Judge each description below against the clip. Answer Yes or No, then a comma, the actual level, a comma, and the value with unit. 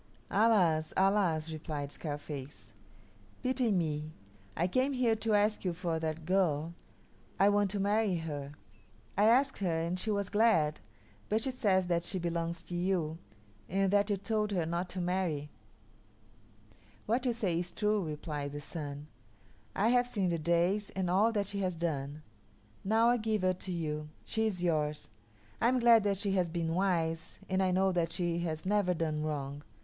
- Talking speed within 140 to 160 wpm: No, average, 175 wpm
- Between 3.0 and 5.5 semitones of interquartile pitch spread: Yes, average, 4.2 semitones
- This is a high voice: No, medium, 180 Hz